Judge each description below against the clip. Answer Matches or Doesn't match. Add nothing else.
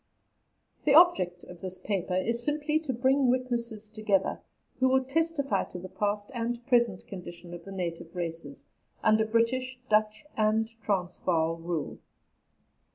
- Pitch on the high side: Matches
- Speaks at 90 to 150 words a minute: Matches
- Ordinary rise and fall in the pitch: Doesn't match